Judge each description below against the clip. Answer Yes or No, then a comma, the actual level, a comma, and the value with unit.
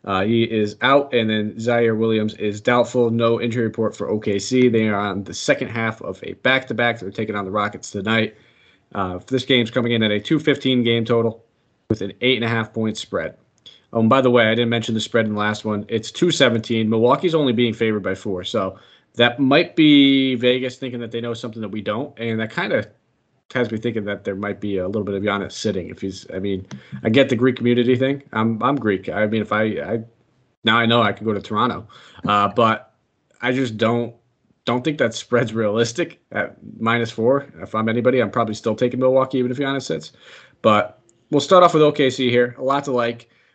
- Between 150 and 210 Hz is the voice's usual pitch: No, low, 115 Hz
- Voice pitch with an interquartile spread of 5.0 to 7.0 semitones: No, narrow, 2.5 semitones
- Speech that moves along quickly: Yes, fast, 220 wpm